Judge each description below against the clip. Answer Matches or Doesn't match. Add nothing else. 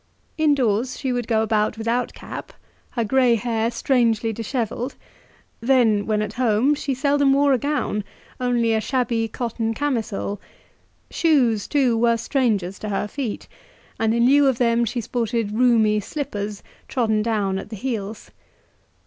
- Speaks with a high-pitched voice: Matches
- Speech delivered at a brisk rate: Doesn't match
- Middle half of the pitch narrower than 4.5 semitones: Matches